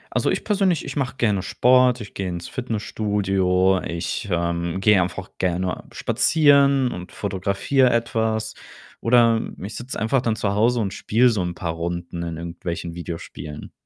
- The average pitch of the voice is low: Yes, low, 100 Hz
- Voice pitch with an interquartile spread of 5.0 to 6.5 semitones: Yes, wide, 5.4 semitones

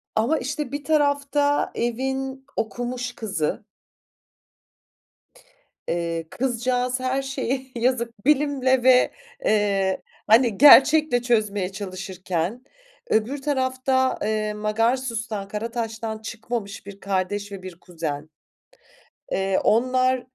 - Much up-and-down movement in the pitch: No, average, 4.3 semitones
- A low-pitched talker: No, high, 235 Hz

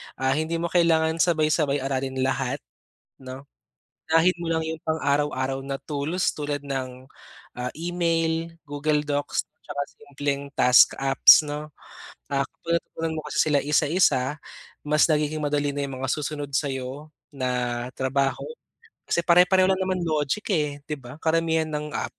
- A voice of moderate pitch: Yes, medium, 145 Hz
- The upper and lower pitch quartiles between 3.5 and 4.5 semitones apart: No, average, 2.9 semitones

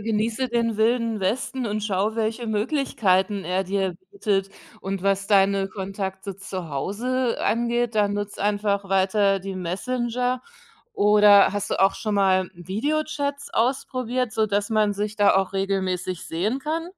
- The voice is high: Yes, high, 205 Hz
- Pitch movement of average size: Yes, average, 3.3 semitones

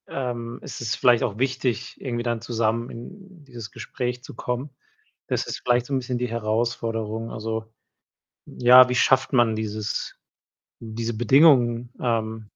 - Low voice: Yes, low, 120 Hz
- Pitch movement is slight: Yes, narrow, 1.8 semitones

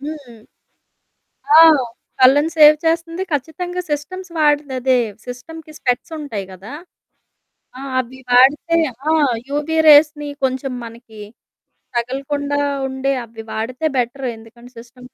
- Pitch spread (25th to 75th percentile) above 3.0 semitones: Yes, average, 3.5 semitones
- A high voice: Yes, very high, 275 Hz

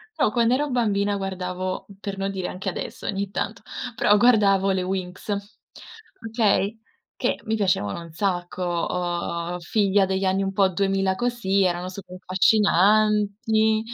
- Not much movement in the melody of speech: Yes, narrow, 2.3 semitones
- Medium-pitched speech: No, high, 195 Hz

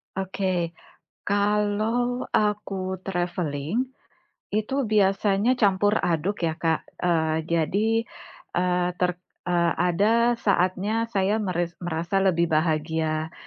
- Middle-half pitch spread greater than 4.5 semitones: No, average, 3.4 semitones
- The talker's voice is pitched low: No, medium, 185 Hz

